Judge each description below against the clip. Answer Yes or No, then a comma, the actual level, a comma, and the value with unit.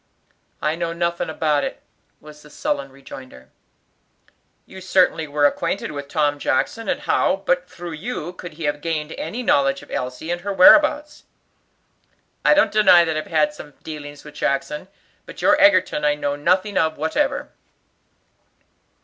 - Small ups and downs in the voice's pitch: No, average, 4.0 semitones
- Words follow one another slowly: No, average, 160 wpm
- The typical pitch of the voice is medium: Yes, medium, 155 Hz